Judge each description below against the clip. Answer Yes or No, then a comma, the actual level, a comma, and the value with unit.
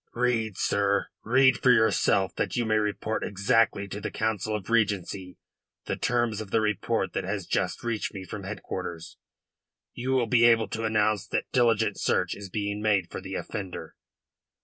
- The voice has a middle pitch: No, low, 105 Hz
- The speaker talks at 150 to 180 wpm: Yes, average, 170 wpm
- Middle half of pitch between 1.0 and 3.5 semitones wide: Yes, narrow, 2.5 semitones